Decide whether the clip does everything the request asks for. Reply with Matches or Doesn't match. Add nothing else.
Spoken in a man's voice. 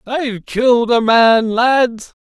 Matches